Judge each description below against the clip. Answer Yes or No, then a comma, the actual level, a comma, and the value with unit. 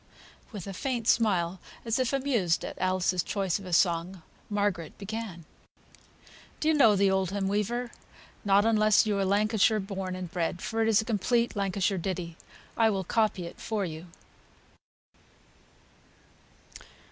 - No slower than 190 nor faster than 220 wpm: No, average, 145 wpm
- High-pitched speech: Yes, high, 200 Hz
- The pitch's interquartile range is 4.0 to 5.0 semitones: No, average, 3.1 semitones